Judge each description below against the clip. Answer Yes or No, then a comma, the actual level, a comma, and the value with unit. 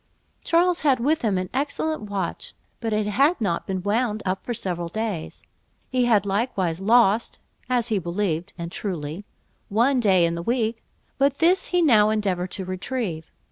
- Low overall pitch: No, high, 210 Hz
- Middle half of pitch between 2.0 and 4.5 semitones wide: No, average, 5.1 semitones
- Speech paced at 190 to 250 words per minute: No, average, 170 wpm